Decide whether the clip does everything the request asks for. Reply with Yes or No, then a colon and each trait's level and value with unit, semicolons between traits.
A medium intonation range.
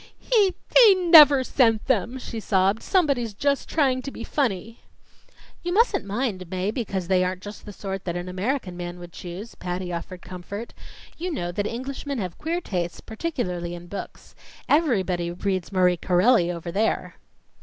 No: wide, 6.7 semitones